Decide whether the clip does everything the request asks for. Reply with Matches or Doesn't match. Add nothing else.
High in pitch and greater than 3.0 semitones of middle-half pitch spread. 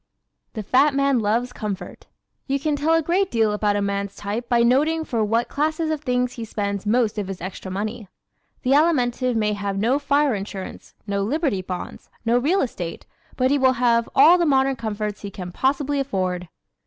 Matches